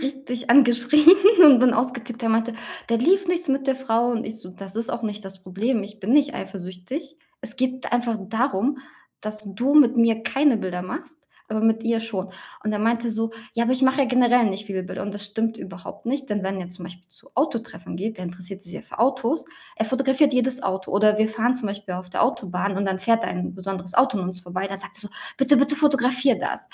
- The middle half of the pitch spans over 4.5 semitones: Yes, average, 4.9 semitones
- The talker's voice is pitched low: No, high, 225 Hz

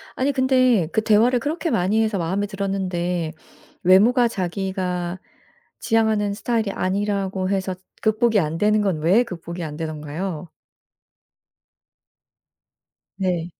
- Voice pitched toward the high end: Yes, high, 195 Hz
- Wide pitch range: No, average, 3.7 semitones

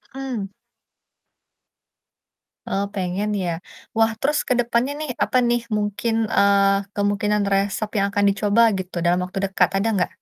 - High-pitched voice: Yes, high, 205 Hz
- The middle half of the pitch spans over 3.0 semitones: No, average, 2.7 semitones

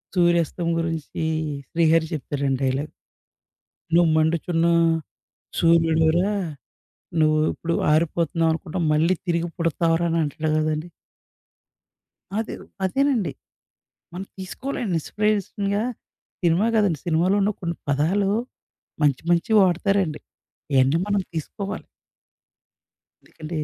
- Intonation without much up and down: No, average, 3.1 semitones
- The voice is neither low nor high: Yes, medium, 170 Hz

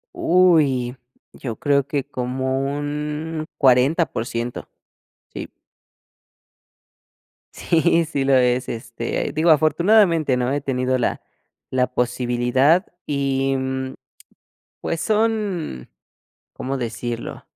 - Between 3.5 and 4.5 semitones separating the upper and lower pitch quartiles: Yes, average, 3.9 semitones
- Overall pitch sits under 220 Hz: Yes, low, 135 Hz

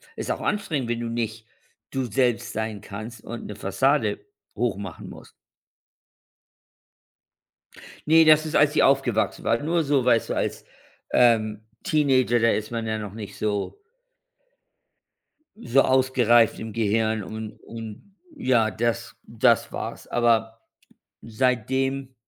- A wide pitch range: No, average, 3.3 semitones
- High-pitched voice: No, low, 115 Hz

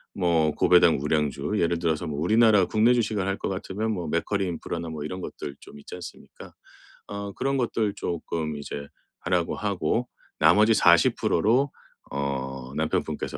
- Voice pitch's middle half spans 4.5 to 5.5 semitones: Yes, average, 5.2 semitones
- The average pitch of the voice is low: Yes, very low, 85 Hz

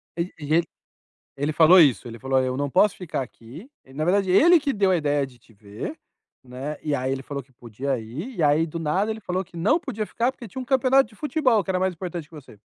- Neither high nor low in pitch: Yes, medium, 160 Hz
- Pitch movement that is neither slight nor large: No, wide, 7.3 semitones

